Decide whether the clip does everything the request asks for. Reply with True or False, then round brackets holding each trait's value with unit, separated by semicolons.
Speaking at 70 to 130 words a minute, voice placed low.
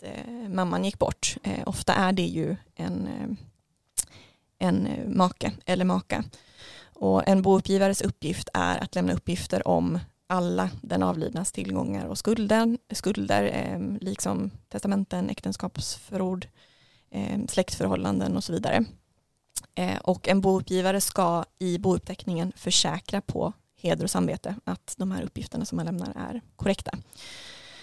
False (125 wpm; 185 Hz)